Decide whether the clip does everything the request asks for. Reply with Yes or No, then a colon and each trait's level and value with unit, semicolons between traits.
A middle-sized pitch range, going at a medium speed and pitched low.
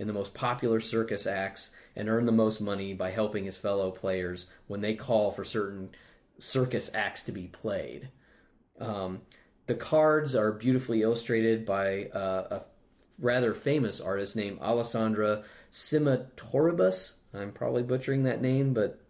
Yes: average, 3.3 semitones; average, 150 wpm; low, 110 Hz